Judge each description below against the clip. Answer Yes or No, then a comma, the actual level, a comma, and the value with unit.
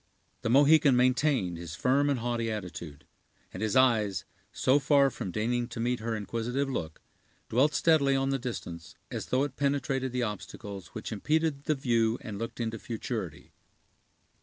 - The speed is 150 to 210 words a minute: Yes, average, 160 wpm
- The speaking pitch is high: No, low, 120 Hz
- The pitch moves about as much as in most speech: Yes, average, 4.1 semitones